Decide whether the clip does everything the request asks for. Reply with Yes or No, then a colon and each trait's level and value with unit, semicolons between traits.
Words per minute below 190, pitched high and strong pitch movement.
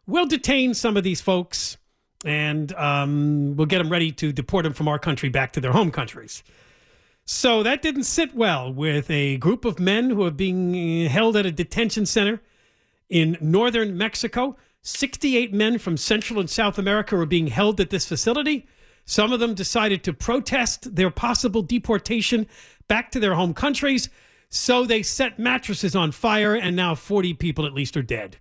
Yes: average, 180 wpm; high, 200 Hz; wide, 5.9 semitones